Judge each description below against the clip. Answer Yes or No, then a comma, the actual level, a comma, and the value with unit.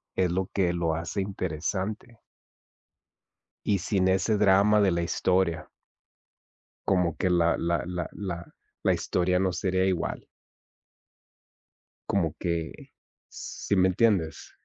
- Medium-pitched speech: No, very low, 95 Hz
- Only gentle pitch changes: Yes, narrow, 2.2 semitones